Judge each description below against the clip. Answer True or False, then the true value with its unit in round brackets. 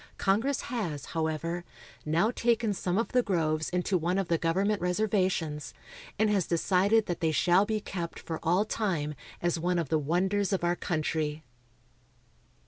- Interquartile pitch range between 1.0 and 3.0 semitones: False (3.9 semitones)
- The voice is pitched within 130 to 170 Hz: False (180 Hz)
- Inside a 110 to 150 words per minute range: False (160 wpm)